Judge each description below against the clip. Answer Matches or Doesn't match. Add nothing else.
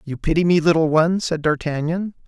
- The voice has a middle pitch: Matches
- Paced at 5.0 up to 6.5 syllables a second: Matches